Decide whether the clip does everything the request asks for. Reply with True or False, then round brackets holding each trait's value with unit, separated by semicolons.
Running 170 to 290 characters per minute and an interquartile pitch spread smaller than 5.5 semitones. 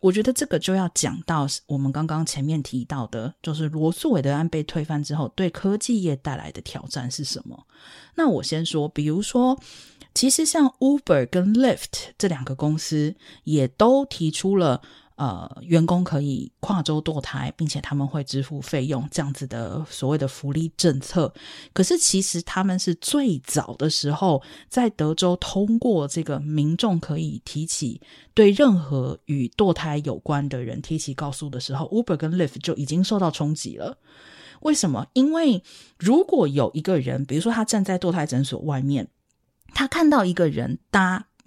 True (275 characters per minute; 5.1 semitones)